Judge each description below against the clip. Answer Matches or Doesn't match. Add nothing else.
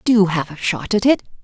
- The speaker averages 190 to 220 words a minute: Doesn't match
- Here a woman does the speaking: Matches